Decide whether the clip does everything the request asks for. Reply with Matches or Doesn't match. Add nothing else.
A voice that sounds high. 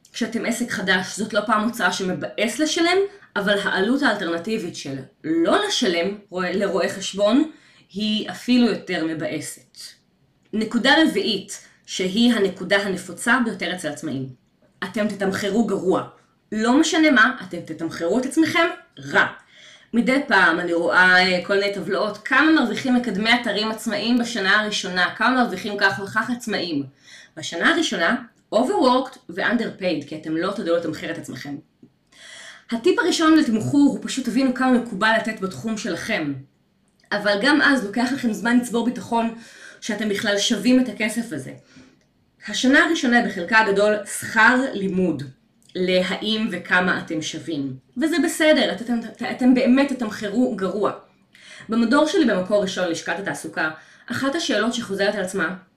Matches